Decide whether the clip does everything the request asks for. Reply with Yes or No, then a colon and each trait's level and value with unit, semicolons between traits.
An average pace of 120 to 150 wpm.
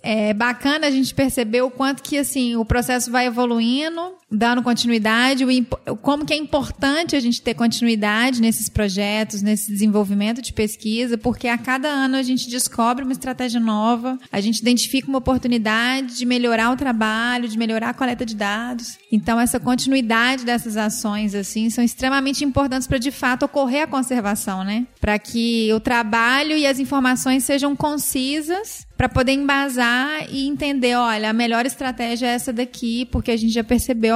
No: average, 170 wpm